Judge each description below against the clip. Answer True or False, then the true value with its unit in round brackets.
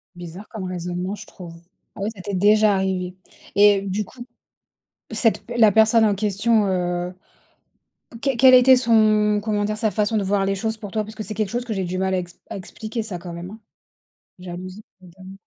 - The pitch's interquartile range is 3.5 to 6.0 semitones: False (2.9 semitones)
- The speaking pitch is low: False (205 Hz)